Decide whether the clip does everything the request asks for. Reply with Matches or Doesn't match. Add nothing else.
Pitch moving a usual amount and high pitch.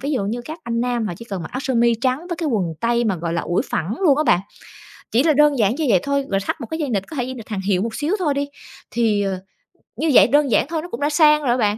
Doesn't match